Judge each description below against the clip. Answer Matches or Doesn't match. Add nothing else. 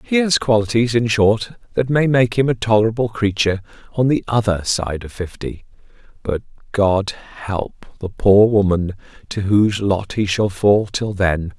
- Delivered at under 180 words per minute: Matches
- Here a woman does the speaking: Doesn't match